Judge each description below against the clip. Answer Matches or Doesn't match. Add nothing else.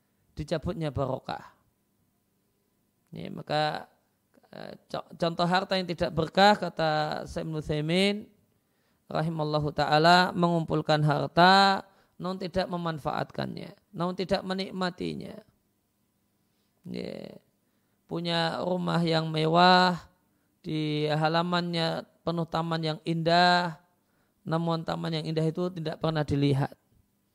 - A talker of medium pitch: Matches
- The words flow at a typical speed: Matches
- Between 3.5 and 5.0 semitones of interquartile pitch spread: Doesn't match